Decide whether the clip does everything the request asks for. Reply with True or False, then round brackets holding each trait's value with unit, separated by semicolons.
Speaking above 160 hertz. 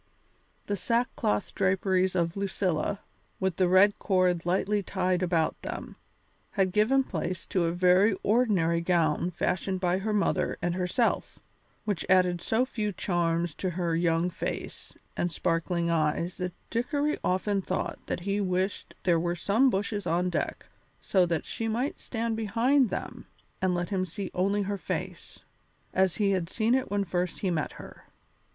True (185 Hz)